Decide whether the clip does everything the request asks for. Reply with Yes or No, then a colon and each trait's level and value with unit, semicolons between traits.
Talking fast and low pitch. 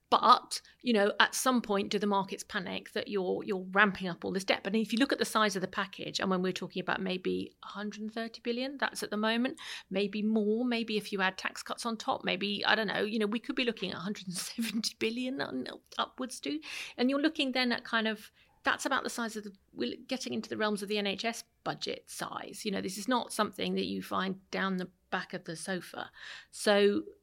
No: fast, 230 wpm; high, 215 Hz